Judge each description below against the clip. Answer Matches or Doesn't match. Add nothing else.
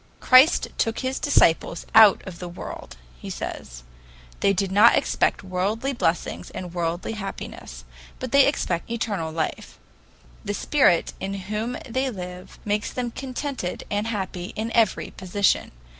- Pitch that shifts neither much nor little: Matches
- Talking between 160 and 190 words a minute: Doesn't match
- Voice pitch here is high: Matches